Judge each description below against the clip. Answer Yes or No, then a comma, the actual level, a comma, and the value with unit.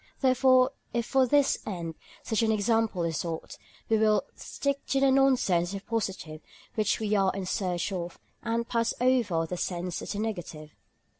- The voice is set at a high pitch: Yes, high, 215 Hz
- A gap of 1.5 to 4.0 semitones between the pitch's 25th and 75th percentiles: No, average, 5.3 semitones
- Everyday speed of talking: Yes, average, 175 wpm